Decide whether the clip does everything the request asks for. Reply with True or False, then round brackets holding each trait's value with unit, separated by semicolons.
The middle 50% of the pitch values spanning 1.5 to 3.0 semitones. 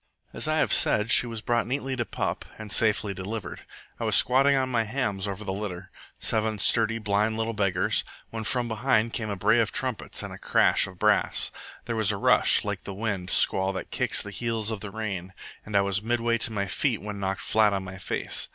True (2.6 semitones)